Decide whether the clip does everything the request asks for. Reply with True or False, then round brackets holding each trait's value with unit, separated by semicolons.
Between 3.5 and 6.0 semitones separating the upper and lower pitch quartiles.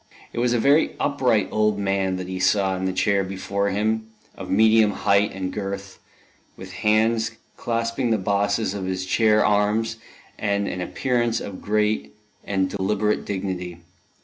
False (2.6 semitones)